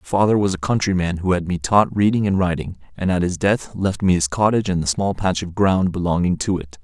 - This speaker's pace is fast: Yes, fast, 255 wpm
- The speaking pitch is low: Yes, very low, 95 Hz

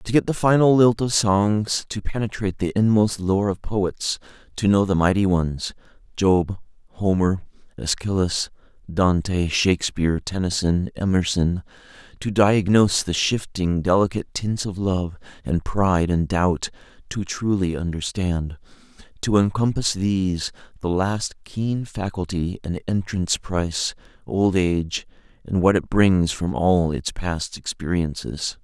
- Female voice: No, male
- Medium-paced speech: No, slow, 130 wpm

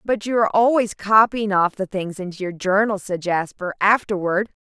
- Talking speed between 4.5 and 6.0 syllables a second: Yes, 5.1 syllables/s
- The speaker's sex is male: No, female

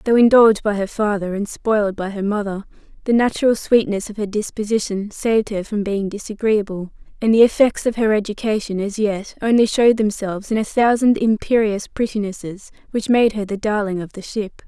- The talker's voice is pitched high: Yes, high, 210 Hz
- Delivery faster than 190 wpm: No, average, 185 wpm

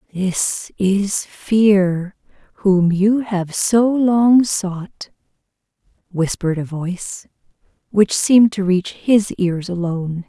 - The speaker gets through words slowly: Yes, slow, 110 wpm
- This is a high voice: Yes, high, 195 Hz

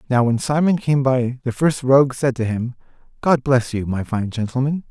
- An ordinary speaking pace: No, fast, 210 wpm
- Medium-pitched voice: No, low, 130 Hz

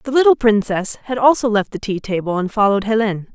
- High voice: Yes, high, 215 Hz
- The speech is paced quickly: Yes, fast, 215 wpm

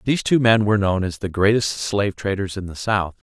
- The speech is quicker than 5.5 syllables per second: Yes, 5.9 syllables/s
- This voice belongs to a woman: No, male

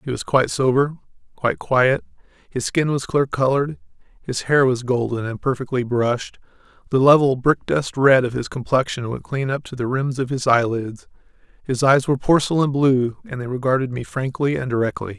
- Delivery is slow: No, average, 185 wpm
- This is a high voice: No, low, 130 Hz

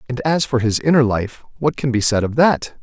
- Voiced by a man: Yes, male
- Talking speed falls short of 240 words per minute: No, fast, 255 wpm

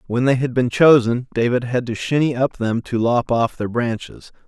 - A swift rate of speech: Yes, fast, 215 wpm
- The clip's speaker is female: No, male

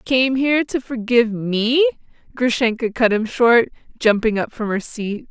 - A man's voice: No, female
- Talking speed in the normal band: Yes, average, 160 wpm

